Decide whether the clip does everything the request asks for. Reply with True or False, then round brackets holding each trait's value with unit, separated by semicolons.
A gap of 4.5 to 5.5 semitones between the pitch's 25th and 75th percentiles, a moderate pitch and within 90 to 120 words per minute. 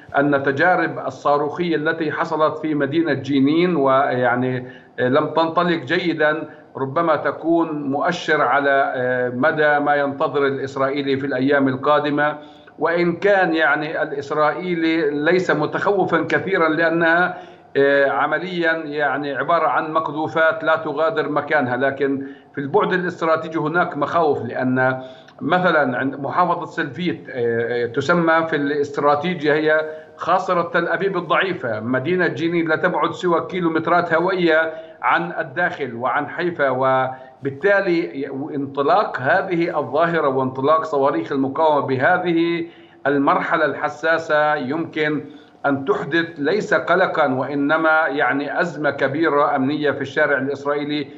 False (2.8 semitones; 150 Hz; 105 wpm)